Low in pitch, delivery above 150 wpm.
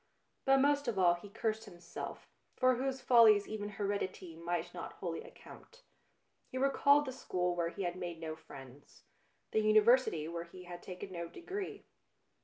No: high, 200 Hz; average, 170 wpm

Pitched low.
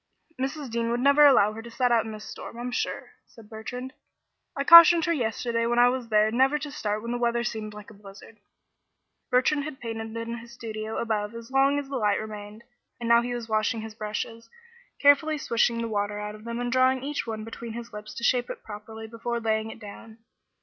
No: high, 230 Hz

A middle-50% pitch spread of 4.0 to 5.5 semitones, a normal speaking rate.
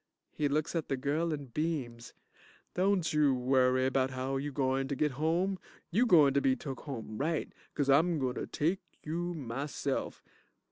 No: average, 3.5 semitones; average, 155 wpm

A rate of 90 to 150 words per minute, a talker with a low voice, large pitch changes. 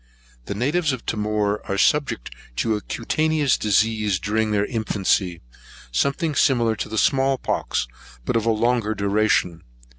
No: average, 140 wpm; low, 110 Hz; average, 3.9 semitones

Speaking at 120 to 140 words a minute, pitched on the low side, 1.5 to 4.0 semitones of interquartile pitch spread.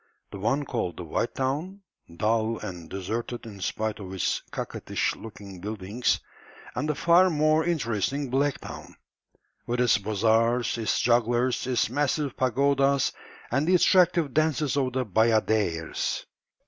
No: slow, 135 wpm; low, 120 Hz; average, 4.7 semitones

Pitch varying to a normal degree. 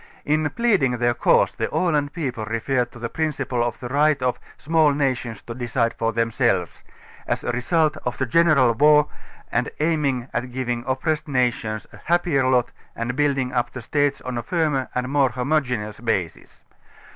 Yes: average, 3.7 semitones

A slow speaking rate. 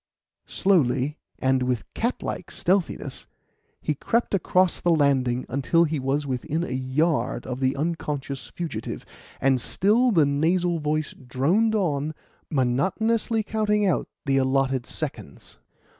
Yes: slow, 130 wpm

